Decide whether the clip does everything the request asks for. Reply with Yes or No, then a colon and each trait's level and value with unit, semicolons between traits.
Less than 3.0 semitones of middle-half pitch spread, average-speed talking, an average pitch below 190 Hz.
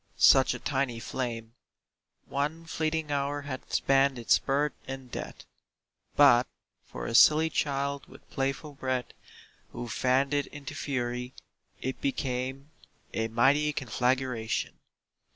No: narrow, 2.4 semitones; slow, 120 wpm; low, 135 Hz